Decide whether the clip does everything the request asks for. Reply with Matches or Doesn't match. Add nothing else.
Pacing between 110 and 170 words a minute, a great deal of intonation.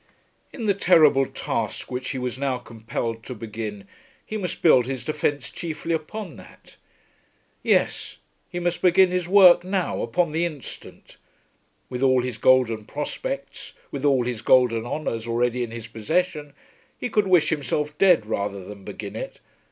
Matches